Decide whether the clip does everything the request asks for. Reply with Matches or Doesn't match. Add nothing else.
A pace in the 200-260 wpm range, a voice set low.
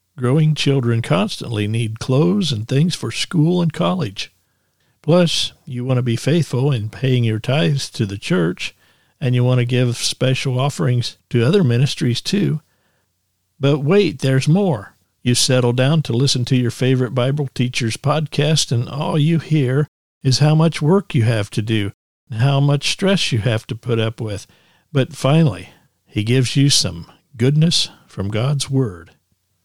Doesn't match